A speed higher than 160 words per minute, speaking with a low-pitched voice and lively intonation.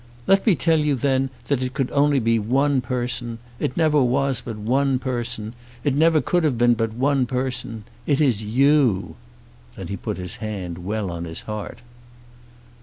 No: average, 180 wpm; low, 125 Hz; average, 4.2 semitones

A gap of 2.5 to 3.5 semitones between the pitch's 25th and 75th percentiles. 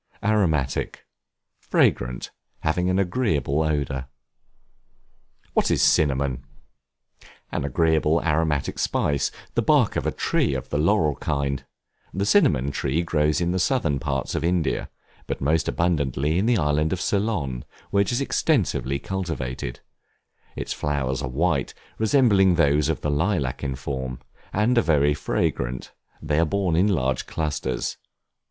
No: average, 4.7 semitones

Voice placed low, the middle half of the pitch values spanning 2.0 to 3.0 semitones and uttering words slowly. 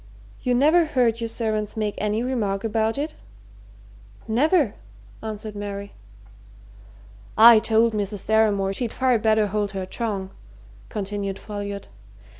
No: high, 215 Hz; narrow, 2.4 semitones; slow, 120 wpm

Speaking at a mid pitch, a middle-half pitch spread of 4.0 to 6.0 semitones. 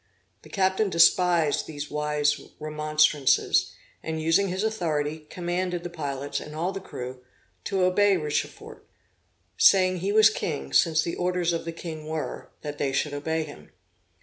No: medium, 160 Hz; average, 3.4 semitones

